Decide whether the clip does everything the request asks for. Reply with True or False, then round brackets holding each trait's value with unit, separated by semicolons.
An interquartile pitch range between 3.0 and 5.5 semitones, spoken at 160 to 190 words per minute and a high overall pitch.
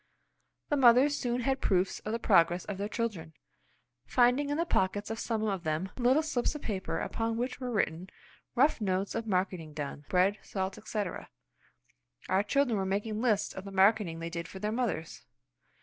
True (4.4 semitones; 180 wpm; 210 Hz)